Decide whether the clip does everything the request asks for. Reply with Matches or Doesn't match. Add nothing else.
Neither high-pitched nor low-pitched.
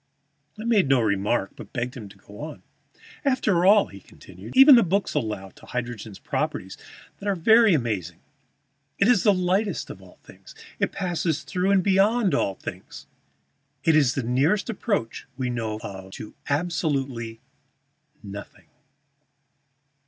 Matches